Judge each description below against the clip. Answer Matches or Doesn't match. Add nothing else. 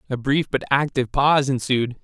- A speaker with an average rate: Matches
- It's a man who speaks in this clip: Matches